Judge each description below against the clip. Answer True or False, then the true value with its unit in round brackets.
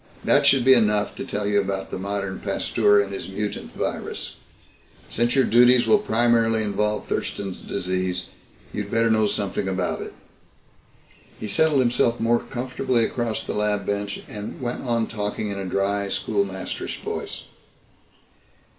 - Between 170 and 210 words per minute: False (150 wpm)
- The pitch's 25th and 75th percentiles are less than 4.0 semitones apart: True (3.0 semitones)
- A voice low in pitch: True (105 Hz)